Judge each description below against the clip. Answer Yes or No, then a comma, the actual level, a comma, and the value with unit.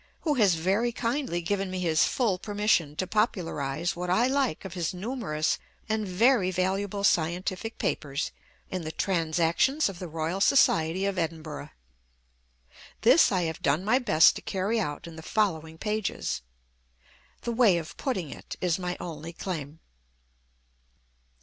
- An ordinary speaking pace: Yes, average, 150 wpm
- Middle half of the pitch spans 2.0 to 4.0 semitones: No, average, 4.6 semitones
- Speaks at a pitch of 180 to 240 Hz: Yes, medium, 185 Hz